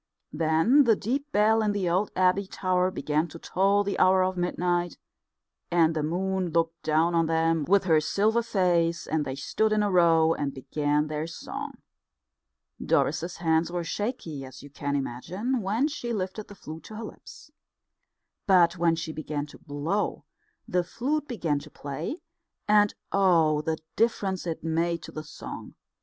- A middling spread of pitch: Yes, average, 4.0 semitones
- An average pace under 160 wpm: No, average, 170 wpm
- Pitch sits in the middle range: Yes, medium, 175 Hz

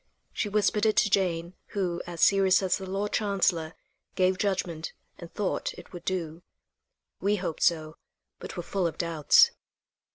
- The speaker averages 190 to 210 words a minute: No, average, 160 wpm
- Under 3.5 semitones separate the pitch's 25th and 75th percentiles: Yes, average, 2.8 semitones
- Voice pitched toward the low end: No, medium, 185 Hz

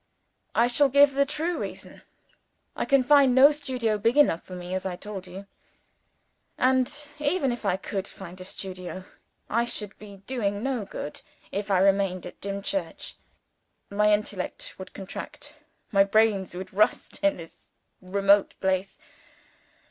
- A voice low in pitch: No, high, 205 Hz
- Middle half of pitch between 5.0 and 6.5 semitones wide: Yes, wide, 5.4 semitones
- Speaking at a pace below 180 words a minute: Yes, average, 155 wpm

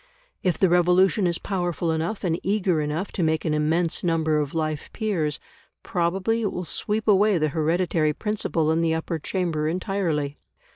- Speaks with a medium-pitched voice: Yes, medium, 170 Hz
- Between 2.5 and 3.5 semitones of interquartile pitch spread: Yes, average, 3.2 semitones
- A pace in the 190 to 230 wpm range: No, average, 165 wpm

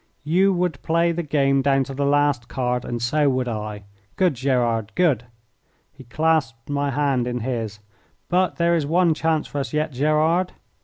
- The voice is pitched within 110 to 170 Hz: Yes, medium, 140 Hz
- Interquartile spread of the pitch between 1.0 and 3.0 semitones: No, average, 4.6 semitones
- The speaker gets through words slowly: No, average, 175 wpm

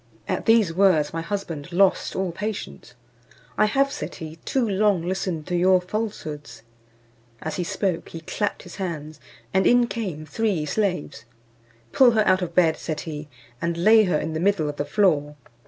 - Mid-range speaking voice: Yes, medium, 180 Hz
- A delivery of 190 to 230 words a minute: No, average, 175 wpm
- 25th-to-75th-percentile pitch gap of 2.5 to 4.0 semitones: No, average, 4.6 semitones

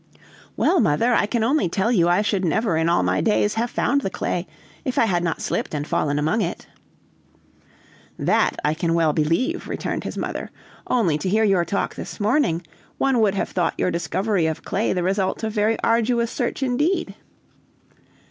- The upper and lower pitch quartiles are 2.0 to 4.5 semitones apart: No, wide, 5.4 semitones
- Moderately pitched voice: No, high, 200 Hz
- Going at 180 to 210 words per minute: Yes, average, 185 wpm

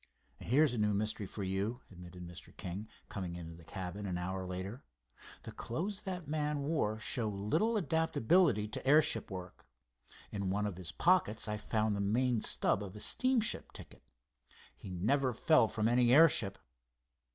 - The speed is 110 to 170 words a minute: Yes, average, 165 wpm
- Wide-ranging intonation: Yes, wide, 7.0 semitones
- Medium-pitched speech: No, low, 110 Hz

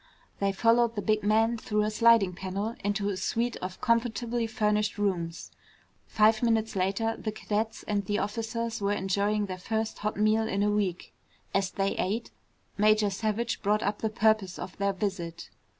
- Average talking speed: Yes, average, 170 wpm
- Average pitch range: No, narrow, 2.0 semitones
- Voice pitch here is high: Yes, high, 210 Hz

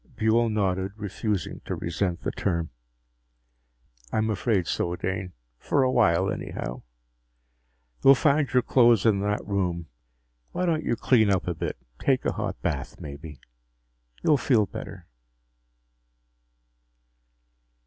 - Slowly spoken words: Yes, slow, 125 wpm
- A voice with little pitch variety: No, average, 4.9 semitones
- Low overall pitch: Yes, low, 100 Hz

